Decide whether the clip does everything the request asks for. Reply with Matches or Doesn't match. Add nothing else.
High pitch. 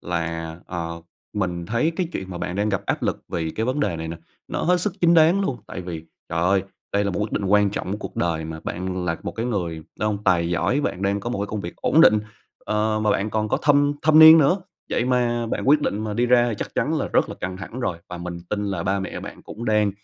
Doesn't match